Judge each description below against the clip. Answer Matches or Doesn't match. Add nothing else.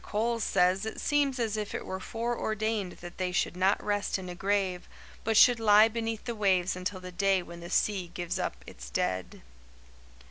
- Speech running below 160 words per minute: Doesn't match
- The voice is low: Doesn't match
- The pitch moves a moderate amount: Matches